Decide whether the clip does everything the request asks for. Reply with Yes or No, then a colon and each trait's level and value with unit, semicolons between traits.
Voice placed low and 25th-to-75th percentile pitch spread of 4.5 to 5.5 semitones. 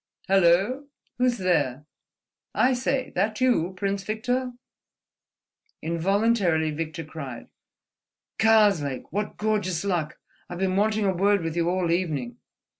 No: high, 190 Hz; average, 4.8 semitones